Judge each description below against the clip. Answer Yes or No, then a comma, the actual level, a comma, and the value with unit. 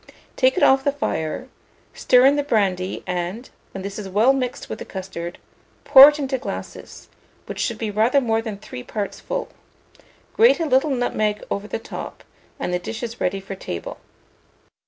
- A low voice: No, high, 225 Hz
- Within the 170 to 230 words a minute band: Yes, average, 180 wpm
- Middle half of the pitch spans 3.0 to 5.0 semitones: No, wide, 5.5 semitones